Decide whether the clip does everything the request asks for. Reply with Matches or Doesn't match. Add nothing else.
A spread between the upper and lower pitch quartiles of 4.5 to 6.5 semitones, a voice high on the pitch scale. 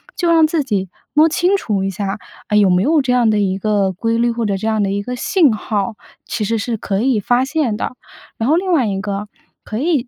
Matches